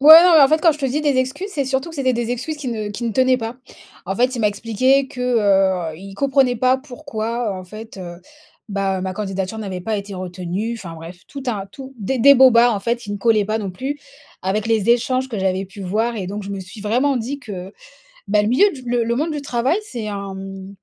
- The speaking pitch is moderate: No, high, 225 Hz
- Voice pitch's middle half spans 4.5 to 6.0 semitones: Yes, average, 4.9 semitones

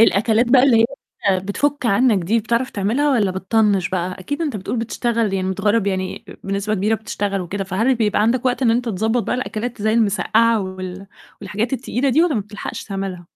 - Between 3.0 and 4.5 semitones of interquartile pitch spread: Yes, average, 3.5 semitones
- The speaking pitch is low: No, high, 215 Hz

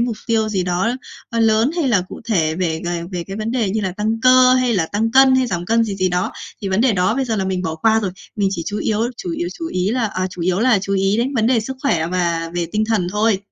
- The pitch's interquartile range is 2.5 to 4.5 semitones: Yes, average, 4.1 semitones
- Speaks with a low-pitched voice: No, high, 210 Hz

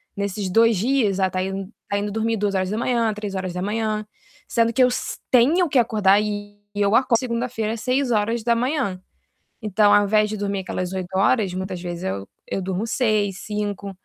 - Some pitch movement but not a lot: Yes, average, 3.0 semitones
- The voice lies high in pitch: Yes, high, 210 Hz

